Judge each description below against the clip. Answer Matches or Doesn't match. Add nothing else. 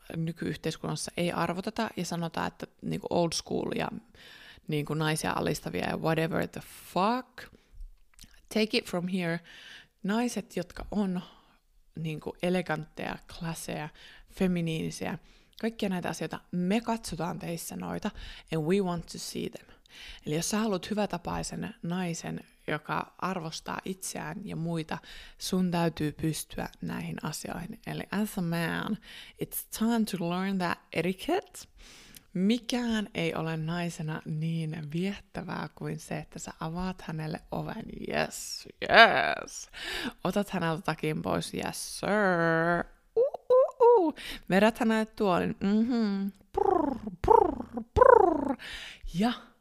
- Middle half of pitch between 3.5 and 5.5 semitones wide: Matches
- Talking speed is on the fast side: Doesn't match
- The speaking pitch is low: Doesn't match